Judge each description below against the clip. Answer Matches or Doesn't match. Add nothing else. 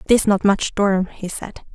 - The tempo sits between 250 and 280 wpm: Doesn't match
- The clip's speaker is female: Matches